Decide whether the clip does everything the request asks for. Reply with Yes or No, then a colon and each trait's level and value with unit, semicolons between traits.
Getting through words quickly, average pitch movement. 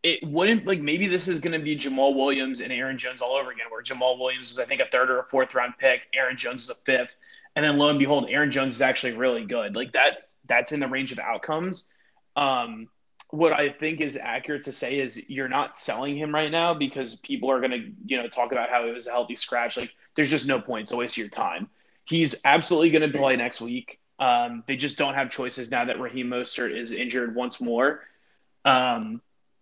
Yes: fast, 235 wpm; average, 3.9 semitones